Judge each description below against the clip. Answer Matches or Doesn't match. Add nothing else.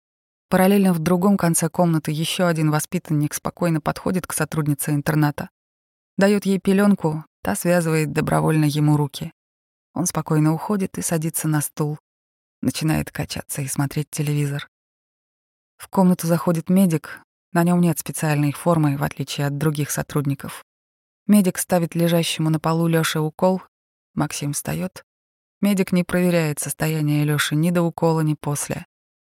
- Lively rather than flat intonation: Doesn't match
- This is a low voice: Doesn't match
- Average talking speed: Matches